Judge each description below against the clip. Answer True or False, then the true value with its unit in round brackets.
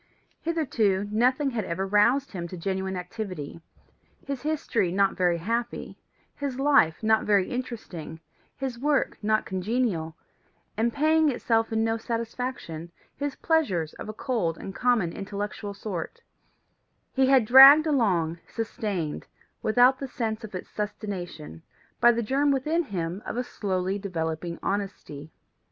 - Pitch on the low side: False (215 Hz)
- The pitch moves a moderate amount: False (5.7 semitones)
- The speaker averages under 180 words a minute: True (140 wpm)